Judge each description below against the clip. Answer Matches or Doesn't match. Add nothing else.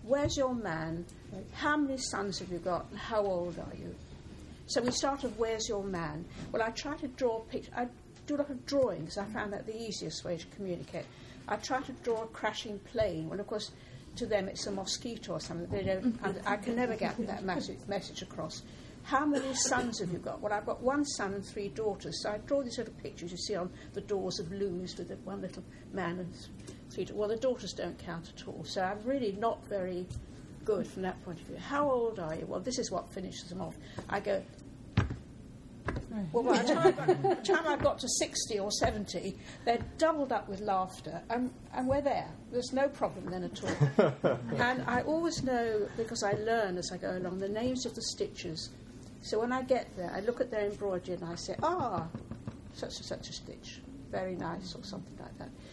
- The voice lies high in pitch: Matches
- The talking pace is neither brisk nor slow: Doesn't match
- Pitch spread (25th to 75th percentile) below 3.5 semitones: Doesn't match